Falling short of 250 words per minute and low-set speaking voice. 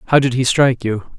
No: fast, 255 wpm; low, 125 Hz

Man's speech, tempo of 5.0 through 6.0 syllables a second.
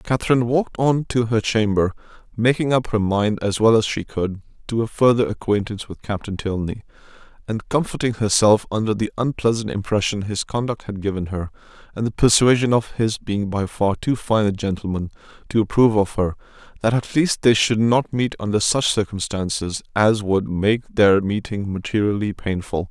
Yes: male; 5.2 syllables/s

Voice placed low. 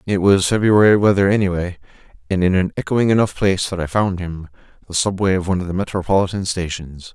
Yes: very low, 95 Hz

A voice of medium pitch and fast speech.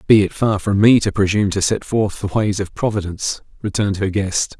No: low, 100 Hz; fast, 220 wpm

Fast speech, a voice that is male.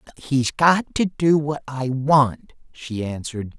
No: average, 150 wpm; male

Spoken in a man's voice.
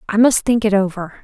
No: female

